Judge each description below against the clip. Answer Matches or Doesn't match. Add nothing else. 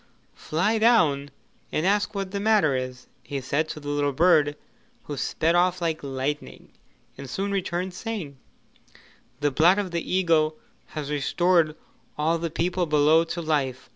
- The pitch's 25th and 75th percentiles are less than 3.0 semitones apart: Doesn't match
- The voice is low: Doesn't match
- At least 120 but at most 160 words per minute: Matches